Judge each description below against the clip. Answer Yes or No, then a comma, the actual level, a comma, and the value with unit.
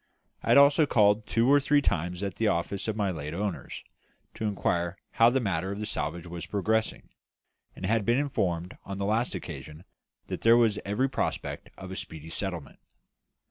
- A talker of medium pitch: No, low, 100 Hz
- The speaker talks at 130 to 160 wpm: No, average, 185 wpm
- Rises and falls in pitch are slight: No, average, 4.7 semitones